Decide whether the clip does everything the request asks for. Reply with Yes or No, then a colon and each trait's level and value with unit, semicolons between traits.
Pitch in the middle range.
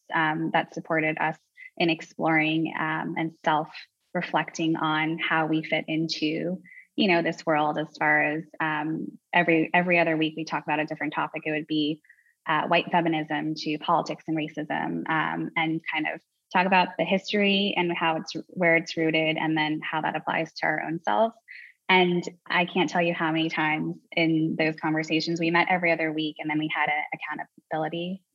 Yes: medium, 160 Hz